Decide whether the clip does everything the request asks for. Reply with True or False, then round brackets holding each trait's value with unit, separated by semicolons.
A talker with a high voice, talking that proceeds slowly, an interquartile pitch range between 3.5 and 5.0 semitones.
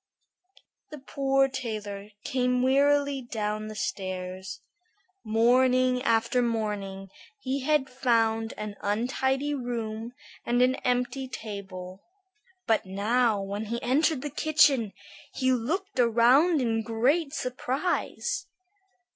True (245 Hz; 105 wpm; 3.8 semitones)